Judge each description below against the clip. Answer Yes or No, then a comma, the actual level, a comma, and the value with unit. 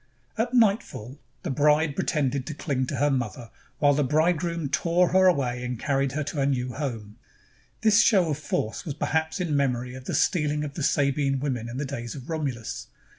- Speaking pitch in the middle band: Yes, medium, 145 Hz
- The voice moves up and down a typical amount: Yes, average, 3.7 semitones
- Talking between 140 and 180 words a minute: No, average, 195 wpm